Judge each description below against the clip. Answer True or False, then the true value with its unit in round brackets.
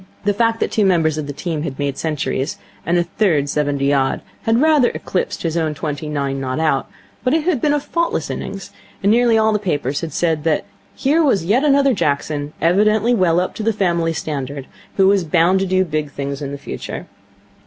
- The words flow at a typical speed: False (210 wpm)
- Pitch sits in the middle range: True (170 Hz)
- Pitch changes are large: True (6.7 semitones)